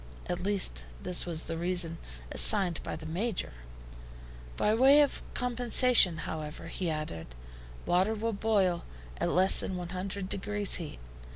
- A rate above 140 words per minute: No, slow, 135 wpm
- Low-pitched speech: No, medium, 185 Hz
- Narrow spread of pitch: No, average, 4.1 semitones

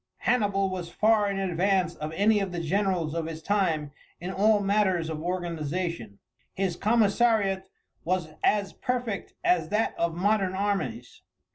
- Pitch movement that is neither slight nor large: Yes, average, 3.4 semitones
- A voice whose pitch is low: No, high, 190 Hz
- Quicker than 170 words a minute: No, average, 145 wpm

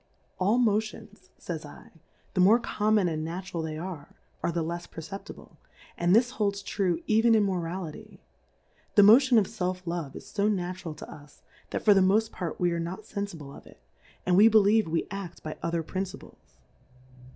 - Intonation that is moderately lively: Yes, average, 3.7 semitones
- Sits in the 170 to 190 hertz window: Yes, medium, 185 Hz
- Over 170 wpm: Yes, average, 180 wpm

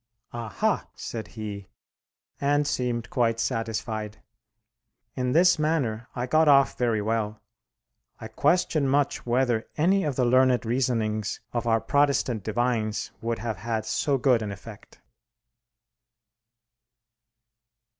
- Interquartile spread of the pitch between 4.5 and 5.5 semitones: No, average, 3.7 semitones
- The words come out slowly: Yes, slow, 115 wpm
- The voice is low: Yes, low, 120 Hz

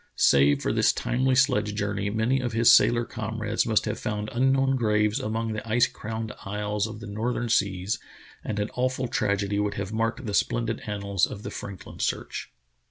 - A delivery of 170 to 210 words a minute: Yes, average, 185 wpm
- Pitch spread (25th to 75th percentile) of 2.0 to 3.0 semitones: Yes, narrow, 2.5 semitones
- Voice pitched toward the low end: Yes, low, 110 Hz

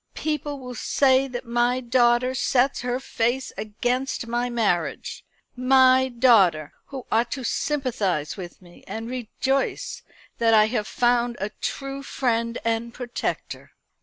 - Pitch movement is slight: Yes, narrow, 2.3 semitones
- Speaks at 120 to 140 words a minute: Yes, slow, 135 wpm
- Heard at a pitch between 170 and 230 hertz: No, high, 245 Hz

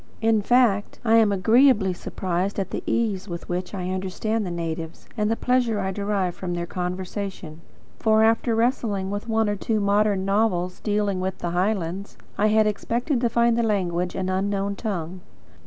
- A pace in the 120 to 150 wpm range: No, average, 175 wpm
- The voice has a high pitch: Yes, high, 200 Hz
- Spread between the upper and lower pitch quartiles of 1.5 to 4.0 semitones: Yes, average, 3.1 semitones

